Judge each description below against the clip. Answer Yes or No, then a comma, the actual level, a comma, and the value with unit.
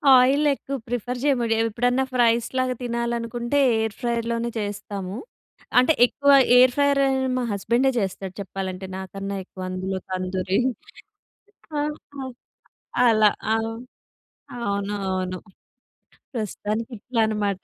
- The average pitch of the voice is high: Yes, high, 225 Hz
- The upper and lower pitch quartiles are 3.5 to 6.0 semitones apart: Yes, average, 3.9 semitones